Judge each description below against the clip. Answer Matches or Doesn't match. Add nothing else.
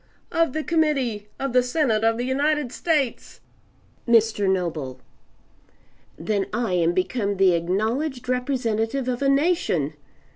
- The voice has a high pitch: Matches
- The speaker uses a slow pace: Matches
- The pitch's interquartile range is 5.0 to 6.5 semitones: Matches